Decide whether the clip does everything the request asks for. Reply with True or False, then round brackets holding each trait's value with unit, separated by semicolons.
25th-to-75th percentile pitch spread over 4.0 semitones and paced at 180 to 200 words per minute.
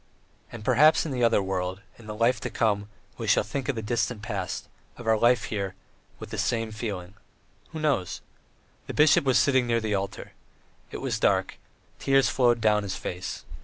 False (3.4 semitones; 190 wpm)